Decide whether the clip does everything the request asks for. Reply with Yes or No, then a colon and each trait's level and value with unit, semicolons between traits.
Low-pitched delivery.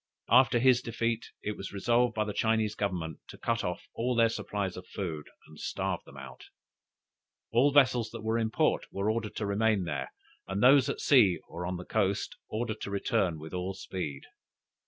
Yes: low, 105 Hz